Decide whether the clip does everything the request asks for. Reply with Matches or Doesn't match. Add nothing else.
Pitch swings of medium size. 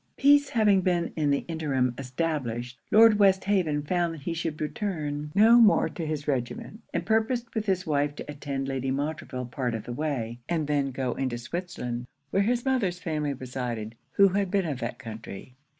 Doesn't match